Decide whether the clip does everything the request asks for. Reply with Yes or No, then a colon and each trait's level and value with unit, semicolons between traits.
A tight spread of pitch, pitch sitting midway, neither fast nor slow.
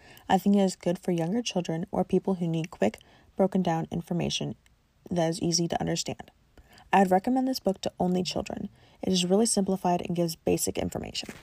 Yes: narrow, 2.3 semitones; medium, 180 Hz; average, 195 wpm